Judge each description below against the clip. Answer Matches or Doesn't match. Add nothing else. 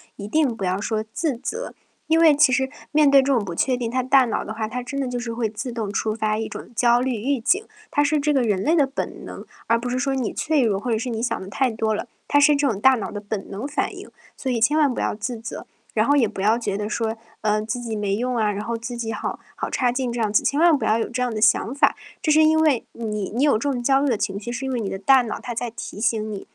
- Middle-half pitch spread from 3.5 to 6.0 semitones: Matches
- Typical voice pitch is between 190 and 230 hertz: Doesn't match